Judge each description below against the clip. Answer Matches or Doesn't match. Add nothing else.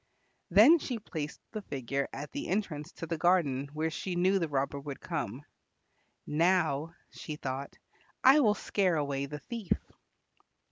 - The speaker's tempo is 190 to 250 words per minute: Doesn't match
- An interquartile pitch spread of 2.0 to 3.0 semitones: Doesn't match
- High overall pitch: Doesn't match